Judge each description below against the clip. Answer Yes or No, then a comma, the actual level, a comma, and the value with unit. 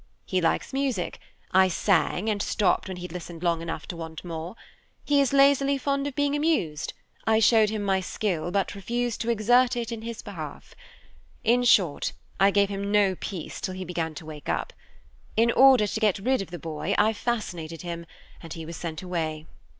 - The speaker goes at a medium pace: Yes, average, 195 wpm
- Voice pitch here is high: Yes, high, 195 Hz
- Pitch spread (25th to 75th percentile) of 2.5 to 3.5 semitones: No, wide, 5.6 semitones